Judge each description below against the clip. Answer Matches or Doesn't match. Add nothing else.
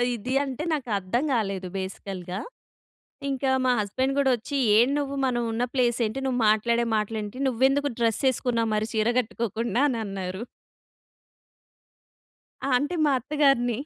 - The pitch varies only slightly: Doesn't match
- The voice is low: Doesn't match